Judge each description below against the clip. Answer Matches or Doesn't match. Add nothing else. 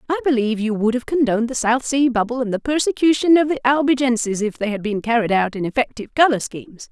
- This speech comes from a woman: Matches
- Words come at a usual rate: Doesn't match